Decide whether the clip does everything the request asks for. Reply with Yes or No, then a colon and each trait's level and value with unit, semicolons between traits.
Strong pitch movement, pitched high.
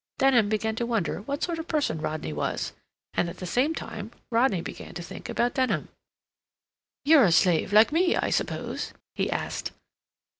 Yes: wide, 7.3 semitones; high, 225 Hz